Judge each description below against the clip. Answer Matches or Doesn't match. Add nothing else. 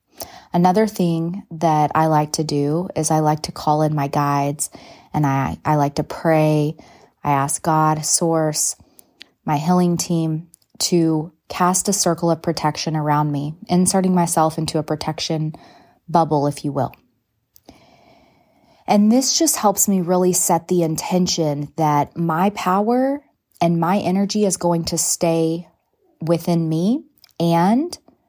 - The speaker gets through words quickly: Doesn't match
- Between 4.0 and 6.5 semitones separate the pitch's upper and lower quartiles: Doesn't match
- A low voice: Doesn't match